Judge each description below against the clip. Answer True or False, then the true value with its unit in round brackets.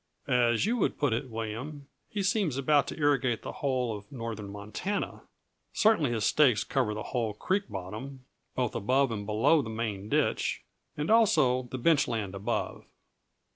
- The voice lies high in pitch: False (125 Hz)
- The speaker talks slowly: False (165 wpm)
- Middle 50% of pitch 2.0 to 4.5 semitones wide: False (5.1 semitones)